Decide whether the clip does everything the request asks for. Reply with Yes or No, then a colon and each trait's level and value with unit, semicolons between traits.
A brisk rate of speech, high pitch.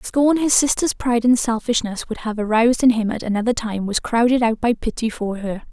Yes: fast, 230 wpm; high, 230 Hz